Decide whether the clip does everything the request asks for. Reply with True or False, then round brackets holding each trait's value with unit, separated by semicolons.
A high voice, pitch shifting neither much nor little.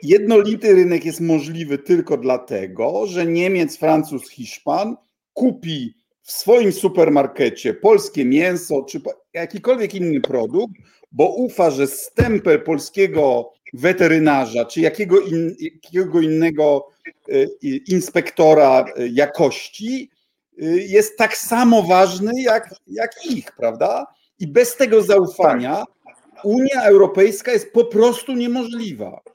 False (195 Hz; 7.3 semitones)